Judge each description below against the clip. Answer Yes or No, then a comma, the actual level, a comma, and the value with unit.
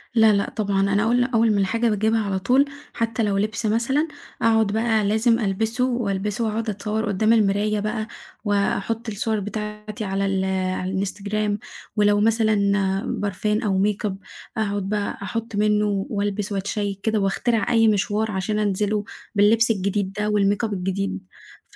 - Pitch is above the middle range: Yes, high, 210 Hz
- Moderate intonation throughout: No, narrow, 1.8 semitones